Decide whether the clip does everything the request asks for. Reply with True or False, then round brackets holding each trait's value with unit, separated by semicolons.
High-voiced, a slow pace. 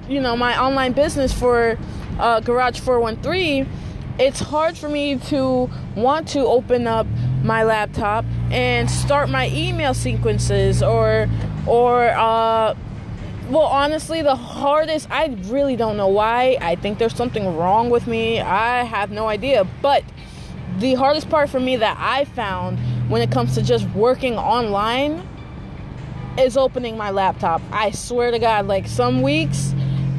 False (230 Hz; 150 wpm)